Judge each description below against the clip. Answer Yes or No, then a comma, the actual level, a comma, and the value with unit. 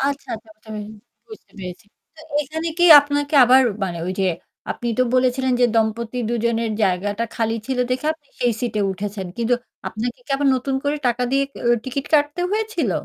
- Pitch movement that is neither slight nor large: Yes, average, 4.1 semitones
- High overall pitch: Yes, high, 245 Hz